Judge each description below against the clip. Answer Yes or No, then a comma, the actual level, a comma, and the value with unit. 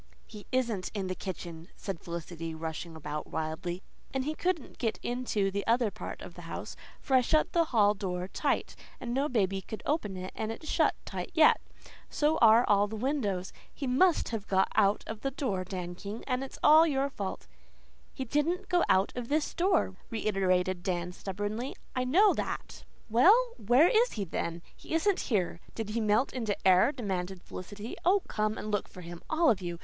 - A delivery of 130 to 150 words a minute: No, average, 190 wpm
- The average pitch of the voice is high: Yes, high, 215 Hz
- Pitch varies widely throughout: Yes, wide, 6.3 semitones